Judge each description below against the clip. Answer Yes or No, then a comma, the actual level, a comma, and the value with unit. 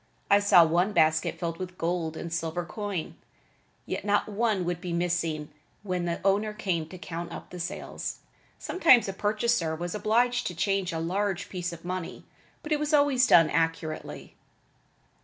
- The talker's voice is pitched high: No, medium, 180 Hz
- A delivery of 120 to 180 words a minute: Yes, average, 170 wpm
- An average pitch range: Yes, average, 3.7 semitones